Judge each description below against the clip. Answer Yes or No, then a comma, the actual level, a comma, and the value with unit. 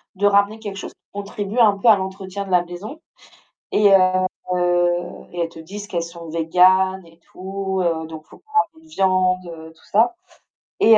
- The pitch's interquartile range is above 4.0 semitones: No, narrow, 2.6 semitones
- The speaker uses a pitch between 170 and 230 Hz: Yes, high, 190 Hz